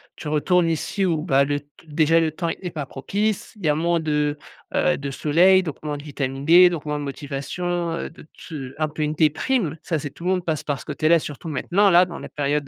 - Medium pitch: Yes, medium, 155 Hz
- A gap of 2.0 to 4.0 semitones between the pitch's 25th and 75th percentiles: Yes, average, 3.0 semitones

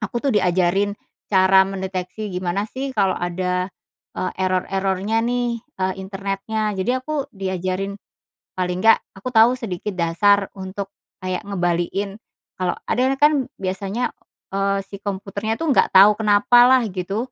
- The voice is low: No, high, 195 Hz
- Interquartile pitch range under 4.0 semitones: Yes, average, 2.9 semitones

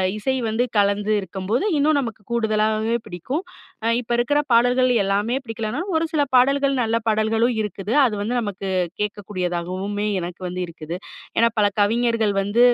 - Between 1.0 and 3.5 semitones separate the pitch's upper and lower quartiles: Yes, average, 3.0 semitones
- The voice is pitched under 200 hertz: No, high, 220 Hz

